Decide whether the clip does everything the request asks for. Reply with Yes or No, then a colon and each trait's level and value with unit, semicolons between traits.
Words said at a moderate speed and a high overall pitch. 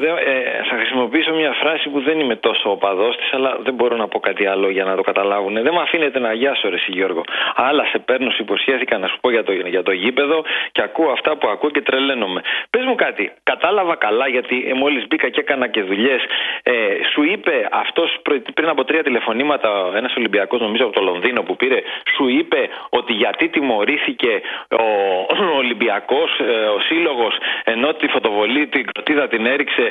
No: fast, 200 wpm; very high, 265 Hz